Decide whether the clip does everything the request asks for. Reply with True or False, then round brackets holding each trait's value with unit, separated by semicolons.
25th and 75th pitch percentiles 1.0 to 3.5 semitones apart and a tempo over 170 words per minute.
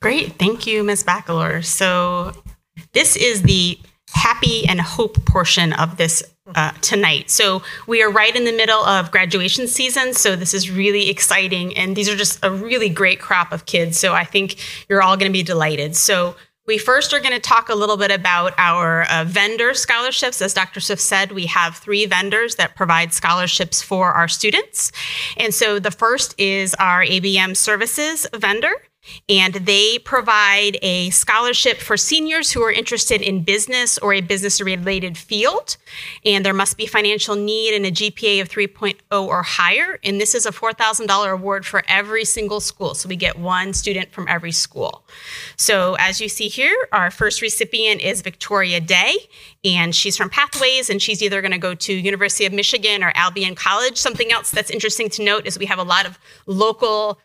True (2.9 semitones; 185 wpm)